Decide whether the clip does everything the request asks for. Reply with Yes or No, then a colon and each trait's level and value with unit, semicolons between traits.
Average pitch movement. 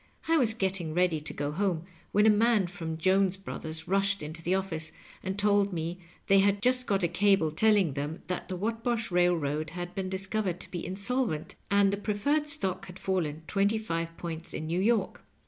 Yes: average, 3.6 semitones